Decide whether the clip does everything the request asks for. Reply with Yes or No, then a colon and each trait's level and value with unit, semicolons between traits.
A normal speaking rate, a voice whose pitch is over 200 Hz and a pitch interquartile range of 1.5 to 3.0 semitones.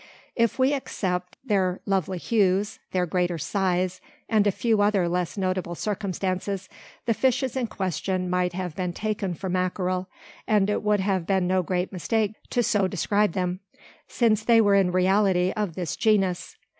No: average, 165 wpm; high, 190 Hz; narrow, 2.6 semitones